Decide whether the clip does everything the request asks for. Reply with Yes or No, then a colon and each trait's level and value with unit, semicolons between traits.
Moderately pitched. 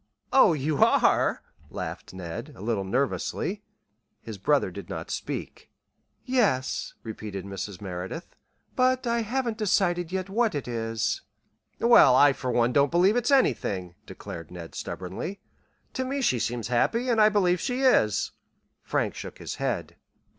Yes: medium, 145 Hz